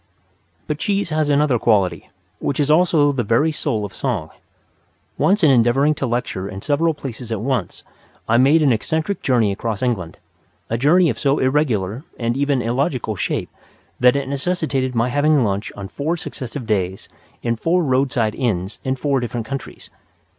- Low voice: Yes, low, 130 Hz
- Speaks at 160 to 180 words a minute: Yes, average, 170 wpm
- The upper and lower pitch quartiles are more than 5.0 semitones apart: No, average, 4.4 semitones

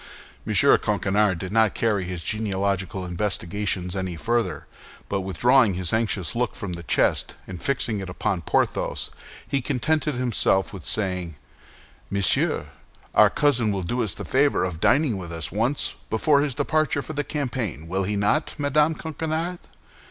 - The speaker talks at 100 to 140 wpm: No, average, 155 wpm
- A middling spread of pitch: No, wide, 6.3 semitones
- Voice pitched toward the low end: Yes, low, 105 Hz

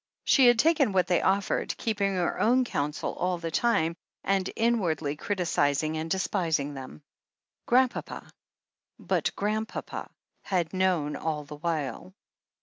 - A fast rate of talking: No, average, 140 wpm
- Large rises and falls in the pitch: No, average, 5.0 semitones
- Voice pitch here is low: No, medium, 180 Hz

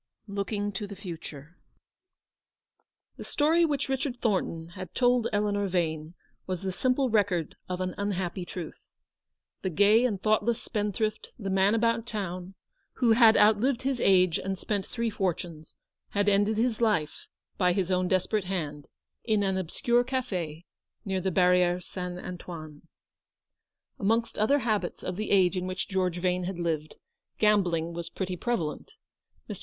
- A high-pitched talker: Yes, high, 195 Hz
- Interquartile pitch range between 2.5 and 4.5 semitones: Yes, average, 3.4 semitones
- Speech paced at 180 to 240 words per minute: No, average, 155 wpm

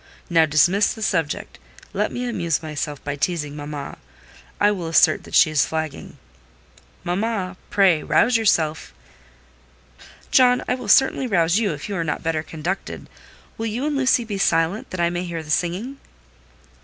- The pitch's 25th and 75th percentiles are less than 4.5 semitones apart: No, average, 5.3 semitones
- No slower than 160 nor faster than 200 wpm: Yes, average, 165 wpm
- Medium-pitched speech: Yes, medium, 175 Hz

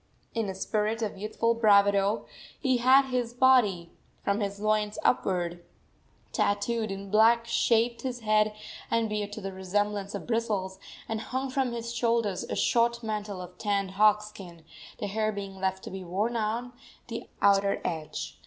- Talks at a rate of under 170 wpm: Yes, average, 160 wpm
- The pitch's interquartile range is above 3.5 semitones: No, average, 2.8 semitones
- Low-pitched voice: No, high, 210 Hz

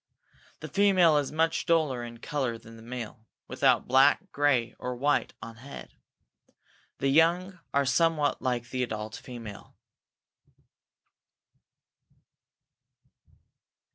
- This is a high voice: No, low, 135 Hz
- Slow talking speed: Yes, slow, 110 wpm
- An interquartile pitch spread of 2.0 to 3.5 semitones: No, average, 5.1 semitones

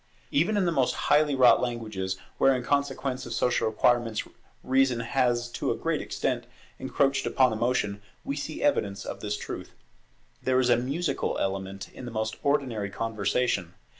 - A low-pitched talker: Yes, low, 125 Hz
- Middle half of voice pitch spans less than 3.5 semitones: No, average, 3.8 semitones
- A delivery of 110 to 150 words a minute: No, average, 165 wpm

